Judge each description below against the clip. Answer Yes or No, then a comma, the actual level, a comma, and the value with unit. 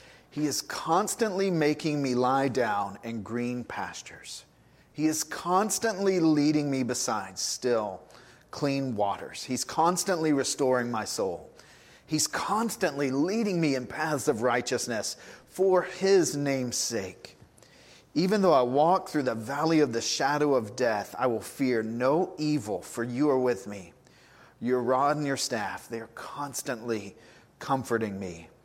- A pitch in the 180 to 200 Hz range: No, medium, 140 Hz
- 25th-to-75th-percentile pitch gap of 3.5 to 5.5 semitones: Yes, average, 4.8 semitones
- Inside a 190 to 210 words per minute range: No, average, 140 wpm